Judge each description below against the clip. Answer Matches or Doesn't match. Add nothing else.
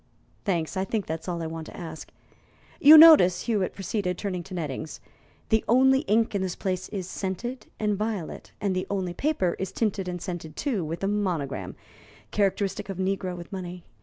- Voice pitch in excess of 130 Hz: Matches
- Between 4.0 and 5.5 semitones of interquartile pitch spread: Doesn't match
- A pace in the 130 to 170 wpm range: Doesn't match